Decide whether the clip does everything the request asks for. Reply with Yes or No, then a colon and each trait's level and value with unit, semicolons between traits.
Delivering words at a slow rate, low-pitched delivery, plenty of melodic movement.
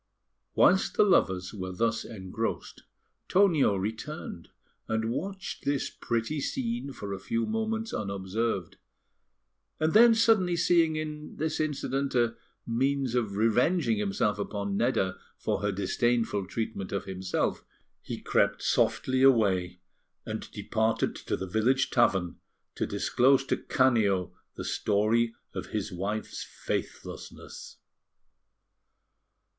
Yes: slow, 120 wpm; low, 115 Hz; wide, 7.0 semitones